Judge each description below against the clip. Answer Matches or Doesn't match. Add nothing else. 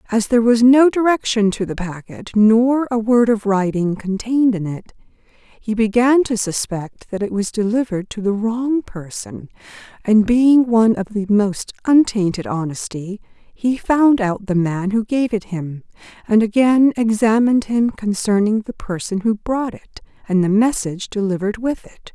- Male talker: Doesn't match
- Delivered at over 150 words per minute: Matches